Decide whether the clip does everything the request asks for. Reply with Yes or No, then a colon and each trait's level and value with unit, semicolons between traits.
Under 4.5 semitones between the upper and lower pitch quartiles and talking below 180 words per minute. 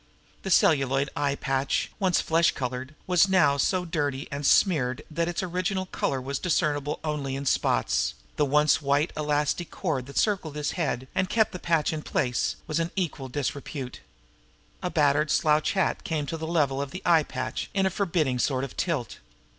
No: average, 3.8 semitones; average, 185 wpm